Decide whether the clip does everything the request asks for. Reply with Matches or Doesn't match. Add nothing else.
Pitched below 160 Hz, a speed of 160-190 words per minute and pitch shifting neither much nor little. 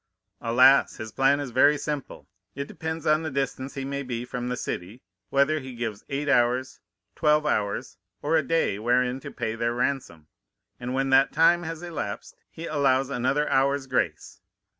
Matches